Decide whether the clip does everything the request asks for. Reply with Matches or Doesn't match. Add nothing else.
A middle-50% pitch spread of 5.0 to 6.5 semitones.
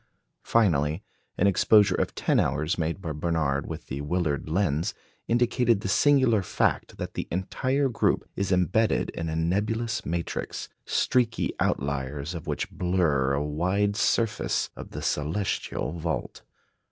Matches